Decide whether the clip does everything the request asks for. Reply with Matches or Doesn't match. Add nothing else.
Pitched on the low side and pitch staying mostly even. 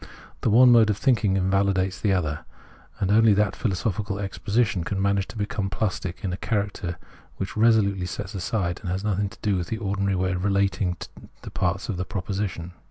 Matches